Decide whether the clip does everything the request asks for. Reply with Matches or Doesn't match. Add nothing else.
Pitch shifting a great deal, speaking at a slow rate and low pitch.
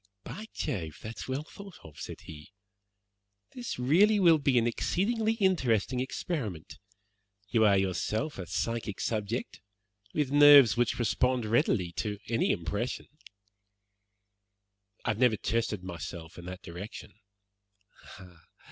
Matches